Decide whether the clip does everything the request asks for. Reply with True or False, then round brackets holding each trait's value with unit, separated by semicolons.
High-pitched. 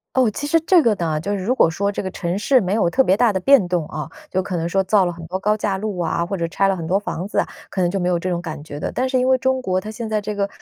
True (195 Hz)